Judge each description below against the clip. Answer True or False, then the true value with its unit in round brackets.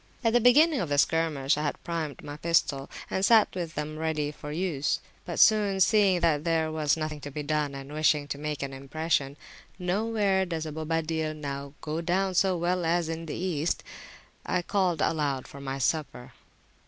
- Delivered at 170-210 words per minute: True (180 wpm)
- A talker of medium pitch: True (160 Hz)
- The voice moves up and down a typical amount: True (3.5 semitones)